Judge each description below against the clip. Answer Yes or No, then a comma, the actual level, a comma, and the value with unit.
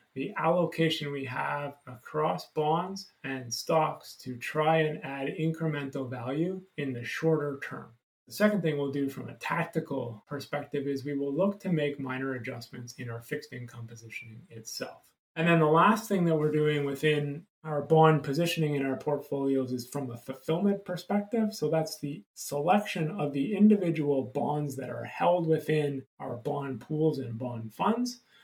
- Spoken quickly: No, average, 165 wpm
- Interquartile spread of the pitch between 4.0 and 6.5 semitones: No, average, 3.3 semitones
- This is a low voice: No, medium, 145 Hz